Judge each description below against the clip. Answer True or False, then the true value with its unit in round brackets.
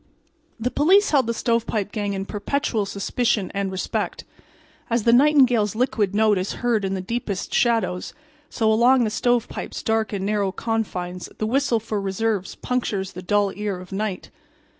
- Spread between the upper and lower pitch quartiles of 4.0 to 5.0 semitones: False (3.2 semitones)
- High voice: True (215 Hz)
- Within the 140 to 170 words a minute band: True (160 wpm)